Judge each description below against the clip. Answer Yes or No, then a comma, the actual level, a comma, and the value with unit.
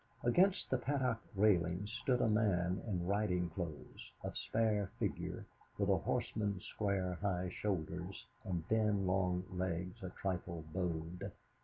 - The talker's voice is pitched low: Yes, very low, 95 Hz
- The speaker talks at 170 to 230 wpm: No, slow, 135 wpm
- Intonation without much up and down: No, average, 3.0 semitones